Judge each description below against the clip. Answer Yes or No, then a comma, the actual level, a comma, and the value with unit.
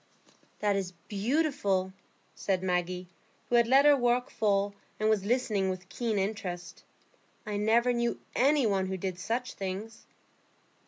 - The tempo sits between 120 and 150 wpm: Yes, average, 145 wpm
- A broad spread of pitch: No, average, 4.0 semitones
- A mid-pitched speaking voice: No, high, 205 Hz